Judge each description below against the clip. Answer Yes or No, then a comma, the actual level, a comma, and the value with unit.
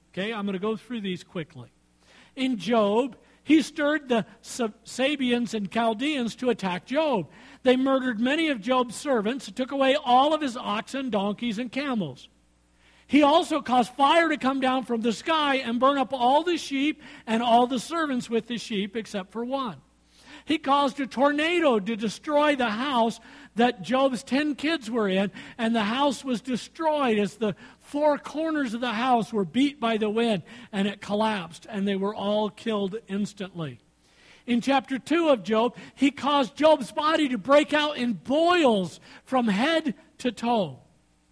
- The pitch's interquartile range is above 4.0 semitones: Yes, average, 4.6 semitones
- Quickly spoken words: No, average, 175 wpm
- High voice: Yes, high, 245 Hz